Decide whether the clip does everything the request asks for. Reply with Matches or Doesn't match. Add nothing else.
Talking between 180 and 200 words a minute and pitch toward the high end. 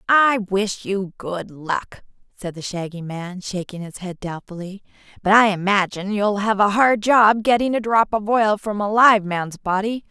Matches